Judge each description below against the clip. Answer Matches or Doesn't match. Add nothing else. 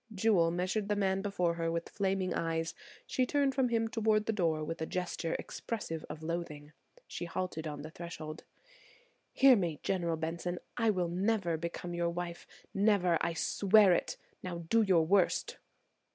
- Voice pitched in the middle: Matches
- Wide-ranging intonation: Doesn't match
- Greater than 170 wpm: Doesn't match